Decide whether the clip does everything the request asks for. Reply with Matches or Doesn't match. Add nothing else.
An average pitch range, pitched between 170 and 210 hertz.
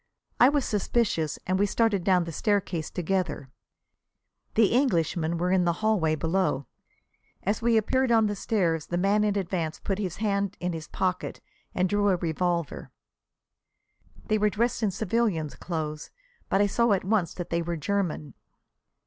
Matches